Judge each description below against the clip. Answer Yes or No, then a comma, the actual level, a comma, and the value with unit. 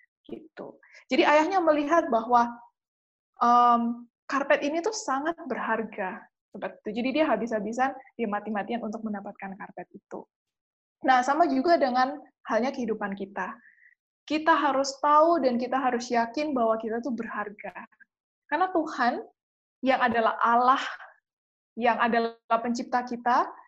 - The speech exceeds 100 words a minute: Yes, average, 120 wpm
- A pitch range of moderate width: Yes, average, 4.6 semitones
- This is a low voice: No, very high, 250 Hz